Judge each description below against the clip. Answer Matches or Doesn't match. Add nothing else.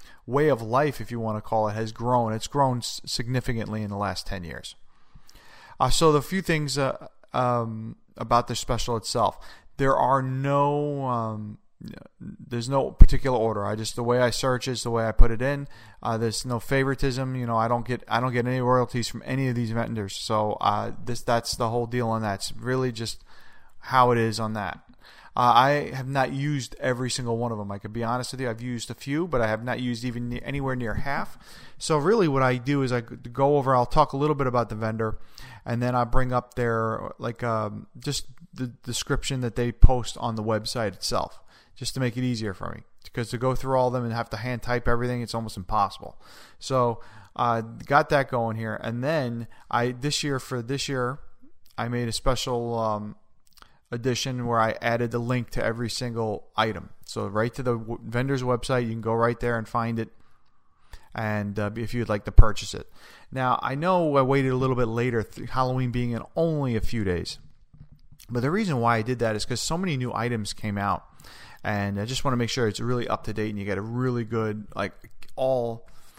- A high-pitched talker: Doesn't match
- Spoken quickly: Matches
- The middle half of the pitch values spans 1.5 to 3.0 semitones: Matches